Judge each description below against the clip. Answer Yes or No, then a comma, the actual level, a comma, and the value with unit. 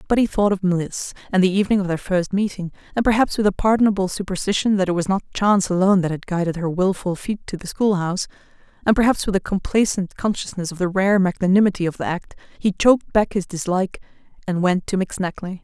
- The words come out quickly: Yes, fast, 210 wpm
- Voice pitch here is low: No, high, 190 Hz